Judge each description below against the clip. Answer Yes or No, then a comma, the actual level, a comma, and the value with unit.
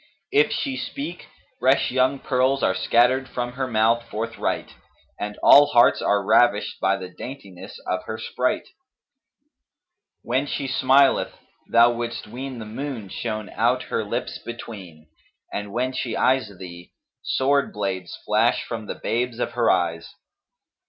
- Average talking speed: Yes, average, 145 wpm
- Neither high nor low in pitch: No, low, 120 Hz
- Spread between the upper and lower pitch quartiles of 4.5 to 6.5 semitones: No, average, 4.0 semitones